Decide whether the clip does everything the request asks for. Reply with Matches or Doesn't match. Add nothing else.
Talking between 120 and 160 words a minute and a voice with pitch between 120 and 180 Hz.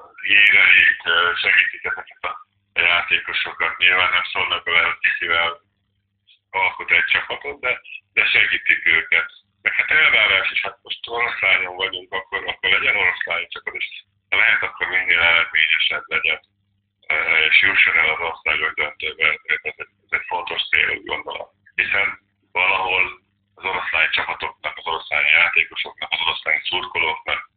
Doesn't match